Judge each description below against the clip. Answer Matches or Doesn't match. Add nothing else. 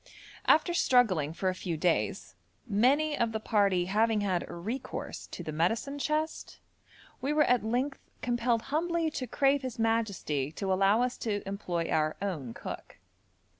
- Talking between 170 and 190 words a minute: Doesn't match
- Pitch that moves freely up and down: Matches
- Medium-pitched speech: Doesn't match